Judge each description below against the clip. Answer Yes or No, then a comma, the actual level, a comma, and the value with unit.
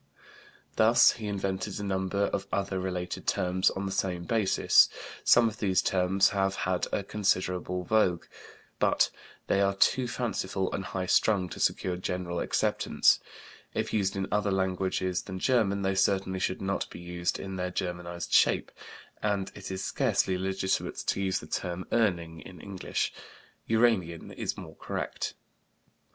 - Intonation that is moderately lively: No, narrow, 1.5 semitones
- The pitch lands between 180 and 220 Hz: No, very low, 95 Hz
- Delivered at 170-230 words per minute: No, average, 155 wpm